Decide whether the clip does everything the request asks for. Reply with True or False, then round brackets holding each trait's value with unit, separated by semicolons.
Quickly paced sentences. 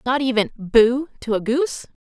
False (175 wpm)